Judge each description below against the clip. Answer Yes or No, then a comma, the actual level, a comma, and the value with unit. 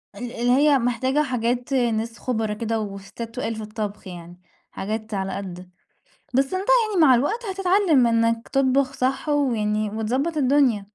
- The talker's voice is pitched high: Yes, high, 235 Hz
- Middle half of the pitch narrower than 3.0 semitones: No, average, 4.1 semitones